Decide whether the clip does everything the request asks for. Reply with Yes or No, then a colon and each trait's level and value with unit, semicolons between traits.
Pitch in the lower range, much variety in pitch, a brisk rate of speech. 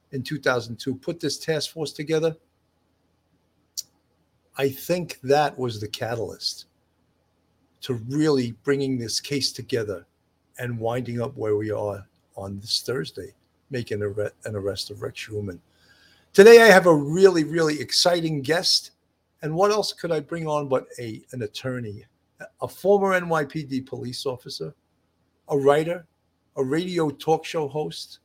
No: low, 130 Hz; wide, 7.5 semitones; average, 140 wpm